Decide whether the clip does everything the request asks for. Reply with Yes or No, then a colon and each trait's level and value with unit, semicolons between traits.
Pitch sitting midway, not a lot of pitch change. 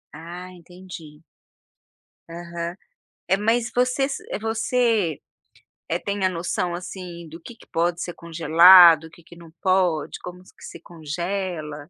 Yes: medium, 175 Hz; narrow, 2.2 semitones